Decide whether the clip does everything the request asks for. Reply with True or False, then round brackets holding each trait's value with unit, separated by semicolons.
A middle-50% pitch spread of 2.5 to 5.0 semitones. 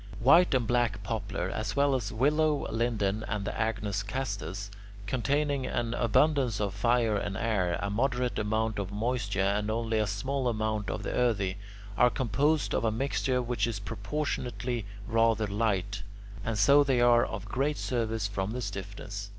True (3.5 semitones)